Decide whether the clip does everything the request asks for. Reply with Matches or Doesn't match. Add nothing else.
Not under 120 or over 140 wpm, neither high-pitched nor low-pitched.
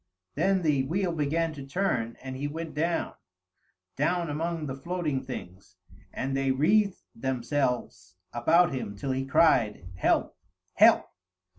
Matches